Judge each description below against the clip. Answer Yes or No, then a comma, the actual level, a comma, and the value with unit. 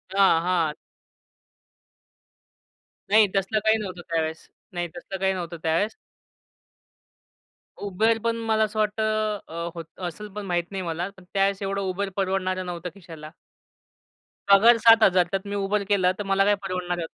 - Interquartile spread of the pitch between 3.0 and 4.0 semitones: No, narrow, 2.6 semitones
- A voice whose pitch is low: No, high, 195 Hz